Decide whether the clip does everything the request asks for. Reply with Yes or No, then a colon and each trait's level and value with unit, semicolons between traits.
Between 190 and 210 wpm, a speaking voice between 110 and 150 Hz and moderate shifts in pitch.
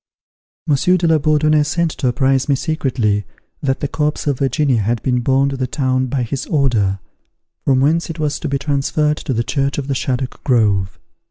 Yes: average, 195 wpm; low, 135 Hz; average, 3.0 semitones